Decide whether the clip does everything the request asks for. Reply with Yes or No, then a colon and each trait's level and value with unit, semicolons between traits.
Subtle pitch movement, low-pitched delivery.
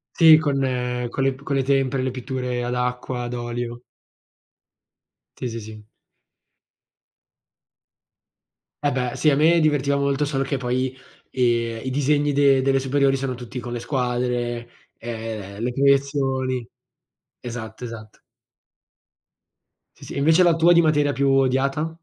Yes: narrow, 2.3 semitones; low, 130 Hz